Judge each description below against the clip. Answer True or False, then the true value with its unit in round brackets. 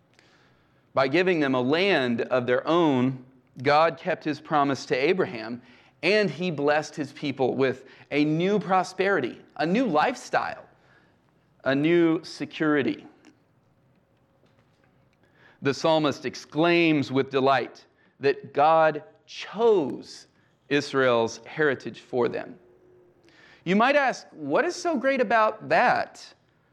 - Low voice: False (155 Hz)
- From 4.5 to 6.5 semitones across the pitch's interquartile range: True (5.4 semitones)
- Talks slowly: True (110 wpm)